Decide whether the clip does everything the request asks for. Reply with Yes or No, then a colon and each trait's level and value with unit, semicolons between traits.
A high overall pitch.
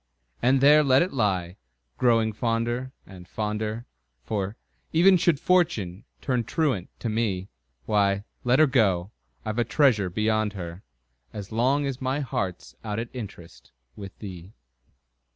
No: low, 110 Hz